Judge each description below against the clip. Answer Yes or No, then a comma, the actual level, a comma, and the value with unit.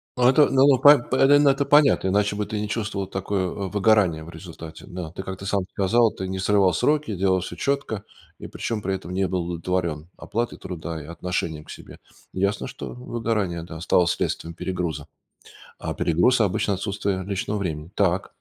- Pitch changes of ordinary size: Yes, average, 3.7 semitones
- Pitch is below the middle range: Yes, very low, 95 Hz